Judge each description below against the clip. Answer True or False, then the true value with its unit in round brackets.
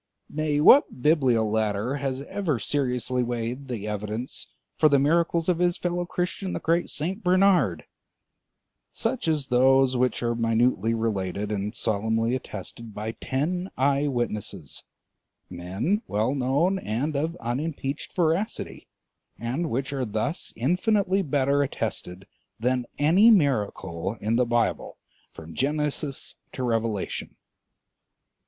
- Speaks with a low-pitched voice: True (130 Hz)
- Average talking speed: False (120 wpm)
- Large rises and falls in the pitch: True (5.9 semitones)